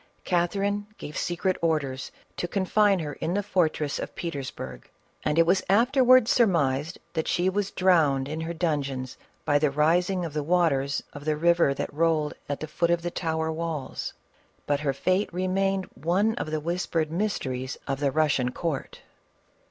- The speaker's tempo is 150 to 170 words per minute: Yes, average, 165 wpm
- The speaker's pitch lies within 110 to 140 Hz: No, medium, 165 Hz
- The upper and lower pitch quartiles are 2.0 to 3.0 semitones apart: No, average, 4.1 semitones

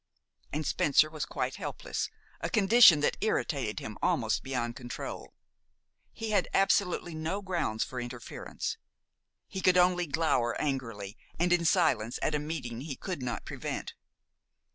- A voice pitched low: No, medium, 155 Hz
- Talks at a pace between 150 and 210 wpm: No, average, 140 wpm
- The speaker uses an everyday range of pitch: No, wide, 6.2 semitones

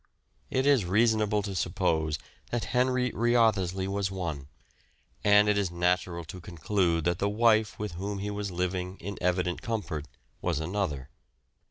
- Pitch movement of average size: Yes, average, 3.2 semitones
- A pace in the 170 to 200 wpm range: No, average, 150 wpm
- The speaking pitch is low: Yes, very low, 95 Hz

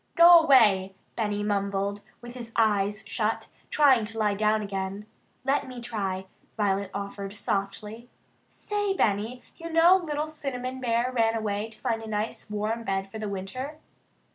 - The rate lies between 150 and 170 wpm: Yes, average, 155 wpm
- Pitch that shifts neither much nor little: Yes, average, 4.0 semitones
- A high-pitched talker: Yes, high, 220 Hz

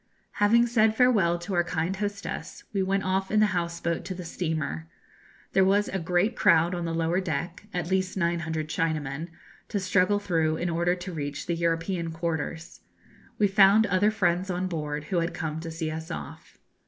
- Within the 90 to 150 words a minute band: No, average, 190 wpm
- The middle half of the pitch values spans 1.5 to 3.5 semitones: Yes, average, 2.8 semitones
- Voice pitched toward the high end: No, medium, 175 Hz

